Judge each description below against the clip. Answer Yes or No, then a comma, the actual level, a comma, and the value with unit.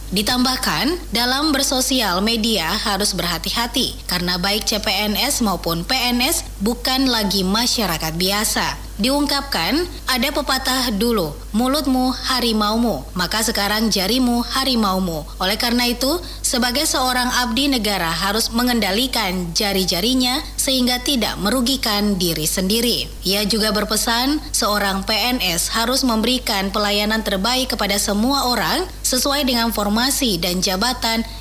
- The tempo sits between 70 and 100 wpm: No, average, 110 wpm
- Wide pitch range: No, average, 4.2 semitones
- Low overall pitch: No, high, 230 Hz